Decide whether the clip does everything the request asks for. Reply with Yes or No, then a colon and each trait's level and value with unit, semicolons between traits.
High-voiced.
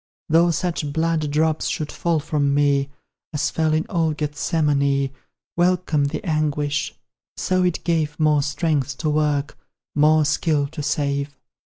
No: medium, 150 Hz